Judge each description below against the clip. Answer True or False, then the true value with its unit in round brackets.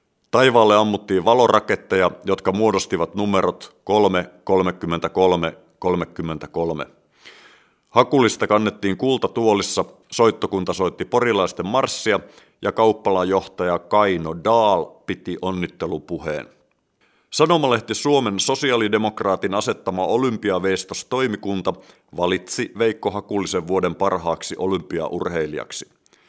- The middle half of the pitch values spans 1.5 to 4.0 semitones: True (3.1 semitones)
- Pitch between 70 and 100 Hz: True (95 Hz)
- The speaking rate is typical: False (75 wpm)